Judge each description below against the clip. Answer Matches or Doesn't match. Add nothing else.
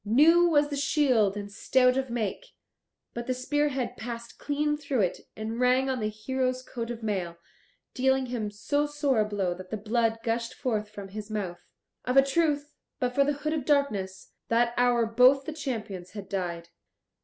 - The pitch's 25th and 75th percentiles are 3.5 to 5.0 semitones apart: Matches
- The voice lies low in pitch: Doesn't match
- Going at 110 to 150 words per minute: Doesn't match